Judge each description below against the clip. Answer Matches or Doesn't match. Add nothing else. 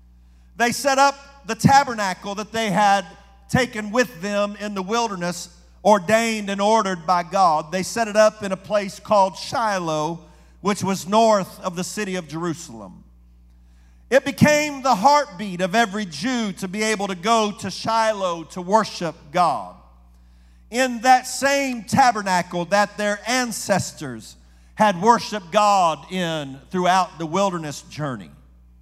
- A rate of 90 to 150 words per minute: Matches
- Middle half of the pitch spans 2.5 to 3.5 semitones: Doesn't match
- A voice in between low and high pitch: Doesn't match